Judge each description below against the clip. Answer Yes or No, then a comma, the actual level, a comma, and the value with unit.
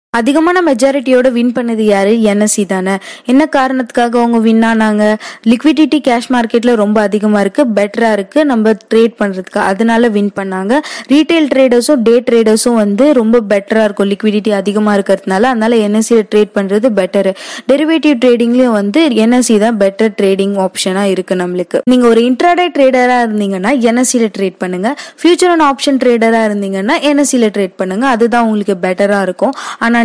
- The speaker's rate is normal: No, fast, 145 wpm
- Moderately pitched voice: No, high, 230 Hz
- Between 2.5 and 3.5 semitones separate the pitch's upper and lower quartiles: No, average, 3.9 semitones